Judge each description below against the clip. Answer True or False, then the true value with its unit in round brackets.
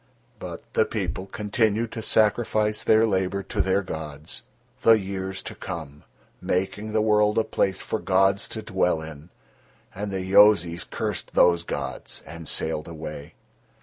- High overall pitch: False (95 Hz)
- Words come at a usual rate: True (150 wpm)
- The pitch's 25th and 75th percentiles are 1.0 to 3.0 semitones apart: False (4.0 semitones)